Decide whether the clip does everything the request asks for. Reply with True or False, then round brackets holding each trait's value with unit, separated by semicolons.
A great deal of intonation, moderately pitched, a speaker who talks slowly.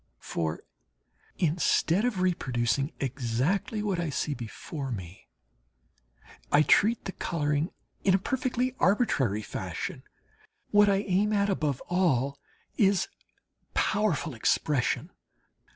True (6.8 semitones; 170 Hz; 105 wpm)